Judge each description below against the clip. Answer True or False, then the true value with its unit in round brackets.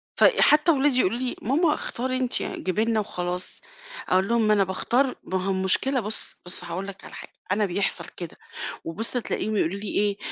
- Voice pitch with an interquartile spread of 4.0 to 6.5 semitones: True (4.9 semitones)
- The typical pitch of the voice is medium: False (210 Hz)